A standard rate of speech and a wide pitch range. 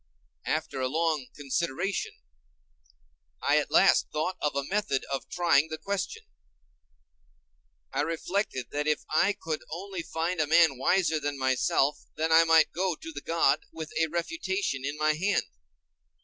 No: average, 150 wpm; average, 3.3 semitones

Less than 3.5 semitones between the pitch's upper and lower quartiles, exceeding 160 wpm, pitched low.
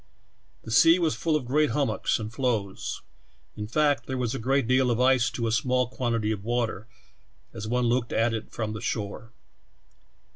Yes: average, 2.8 semitones; average, 190 wpm; low, 120 Hz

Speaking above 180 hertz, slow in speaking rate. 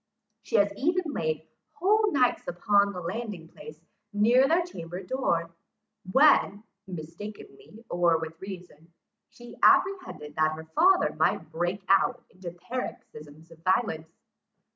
Yes: high, 190 Hz; slow, 125 wpm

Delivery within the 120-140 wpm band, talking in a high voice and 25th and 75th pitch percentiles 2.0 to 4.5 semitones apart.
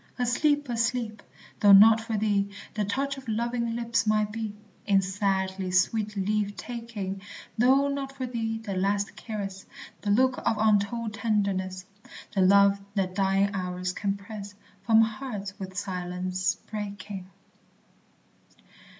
Yes: slow, 135 wpm; high, 205 Hz; average, 2.7 semitones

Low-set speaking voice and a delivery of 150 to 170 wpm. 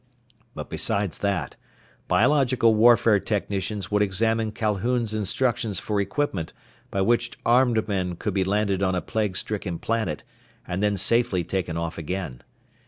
No: low, 105 Hz; average, 140 wpm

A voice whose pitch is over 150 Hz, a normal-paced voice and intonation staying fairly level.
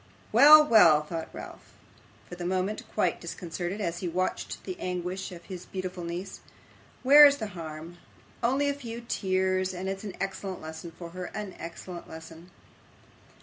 No: medium, 185 Hz; average, 160 wpm; average, 3.3 semitones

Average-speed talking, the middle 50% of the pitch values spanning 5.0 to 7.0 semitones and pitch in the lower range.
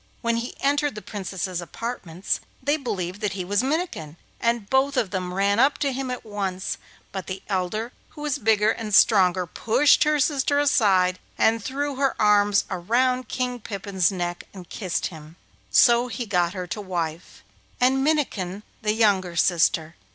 No: average, 165 wpm; wide, 5.5 semitones; high, 210 Hz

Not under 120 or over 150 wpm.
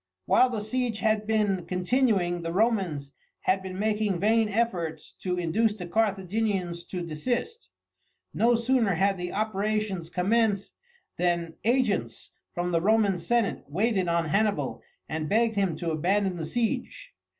Yes: average, 140 wpm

